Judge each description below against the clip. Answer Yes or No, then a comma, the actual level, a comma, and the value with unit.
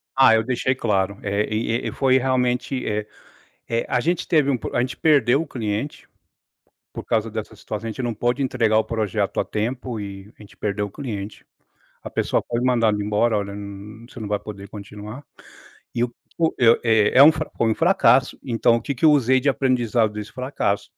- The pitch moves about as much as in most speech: Yes, average, 3.6 semitones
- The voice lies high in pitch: No, low, 115 Hz